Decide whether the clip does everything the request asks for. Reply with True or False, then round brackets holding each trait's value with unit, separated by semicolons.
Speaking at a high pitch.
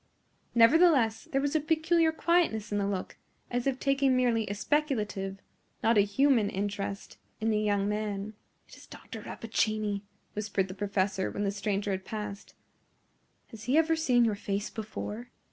True (215 Hz)